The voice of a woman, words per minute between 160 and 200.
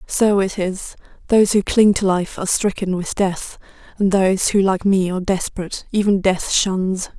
Yes: female; average, 185 wpm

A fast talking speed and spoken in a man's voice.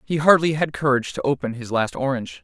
Yes: fast, 220 wpm; male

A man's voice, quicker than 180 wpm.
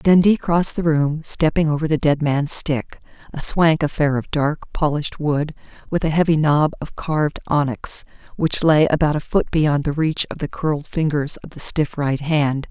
No: female; average, 190 wpm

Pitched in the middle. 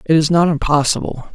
Yes: medium, 155 Hz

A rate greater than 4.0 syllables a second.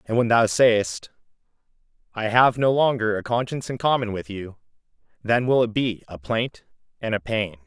Yes: 5.0 syllables/s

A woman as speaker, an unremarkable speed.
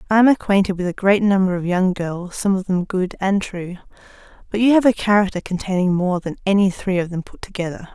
No: female; fast, 225 wpm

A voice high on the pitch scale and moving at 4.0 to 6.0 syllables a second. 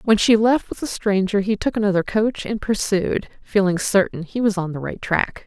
Yes: high, 205 Hz; 5.0 syllables/s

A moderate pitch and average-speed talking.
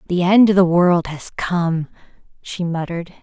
Yes: medium, 175 Hz; average, 165 wpm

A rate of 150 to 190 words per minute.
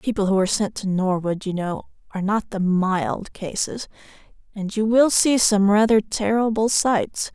Yes: average, 180 wpm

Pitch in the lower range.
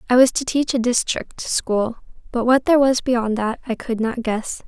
No: high, 240 Hz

